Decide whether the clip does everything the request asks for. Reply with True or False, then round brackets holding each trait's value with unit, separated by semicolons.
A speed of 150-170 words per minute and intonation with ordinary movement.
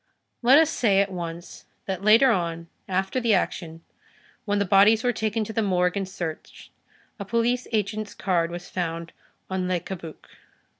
True (165 wpm; 3.8 semitones)